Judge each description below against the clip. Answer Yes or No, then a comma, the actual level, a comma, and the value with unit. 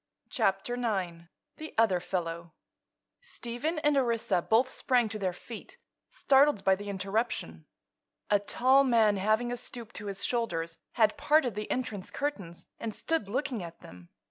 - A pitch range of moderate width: Yes, average, 4.7 semitones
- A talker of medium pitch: No, high, 220 Hz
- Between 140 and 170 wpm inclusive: Yes, average, 150 wpm